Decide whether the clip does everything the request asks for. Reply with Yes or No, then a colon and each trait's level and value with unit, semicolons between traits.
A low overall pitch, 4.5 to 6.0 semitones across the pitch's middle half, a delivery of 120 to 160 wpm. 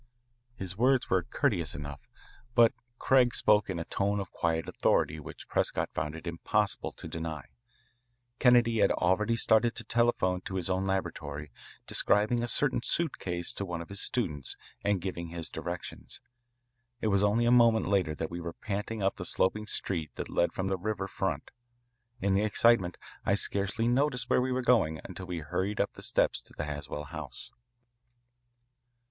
No: very low, 95 Hz; average, 5.0 semitones; average, 175 wpm